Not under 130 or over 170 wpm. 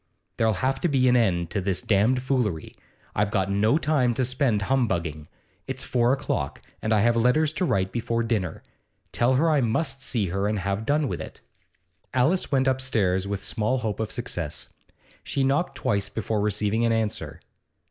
No: average, 180 wpm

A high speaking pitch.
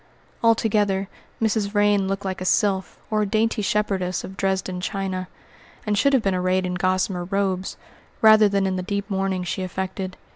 Yes: high, 195 Hz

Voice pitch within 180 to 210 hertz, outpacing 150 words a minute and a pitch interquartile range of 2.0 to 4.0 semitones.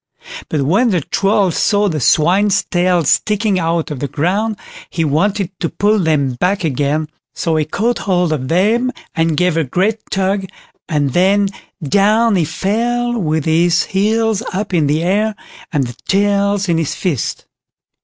No: medium, 185 Hz; average, 165 wpm; average, 4.4 semitones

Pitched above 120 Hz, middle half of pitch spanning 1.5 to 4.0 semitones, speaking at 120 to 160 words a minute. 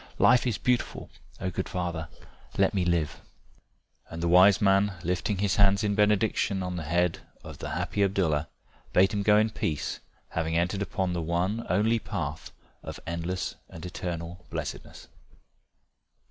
No: very low, 90 Hz; average, 3.1 semitones; average, 155 wpm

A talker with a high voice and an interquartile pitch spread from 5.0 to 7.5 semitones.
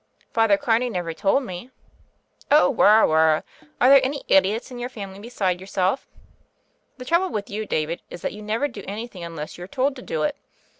Yes: high, 210 Hz; wide, 5.4 semitones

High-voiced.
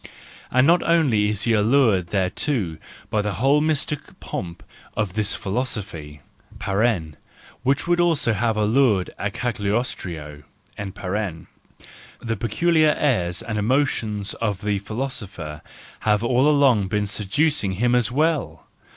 No: low, 110 Hz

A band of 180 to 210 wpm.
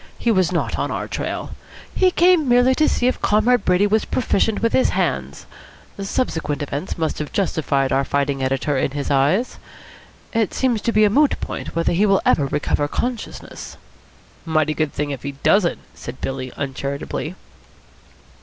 No: average, 170 wpm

